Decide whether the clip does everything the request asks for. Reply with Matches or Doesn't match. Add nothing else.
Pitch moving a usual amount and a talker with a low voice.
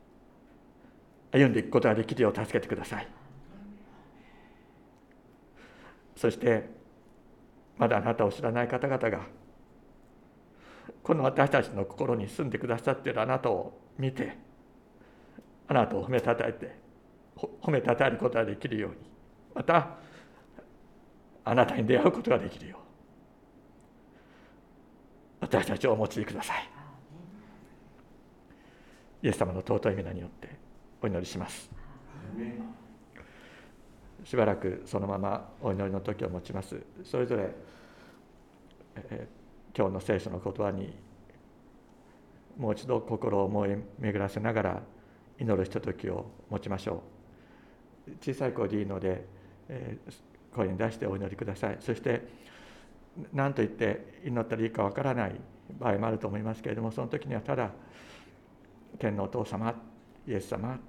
Matches